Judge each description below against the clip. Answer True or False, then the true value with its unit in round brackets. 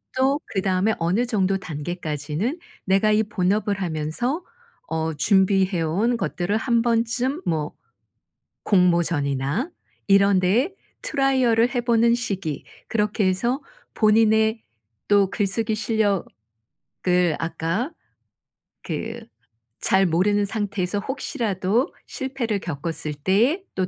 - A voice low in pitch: False (200 Hz)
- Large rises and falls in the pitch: False (4.7 semitones)